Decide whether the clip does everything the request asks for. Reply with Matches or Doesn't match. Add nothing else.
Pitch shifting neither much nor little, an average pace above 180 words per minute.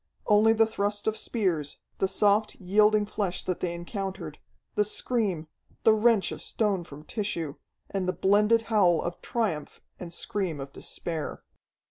Doesn't match